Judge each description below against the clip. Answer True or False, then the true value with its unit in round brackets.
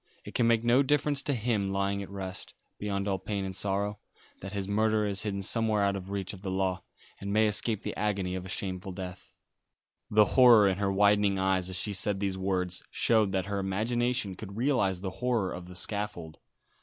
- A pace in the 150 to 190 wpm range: False (205 wpm)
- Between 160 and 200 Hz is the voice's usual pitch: False (100 Hz)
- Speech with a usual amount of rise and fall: False (2.1 semitones)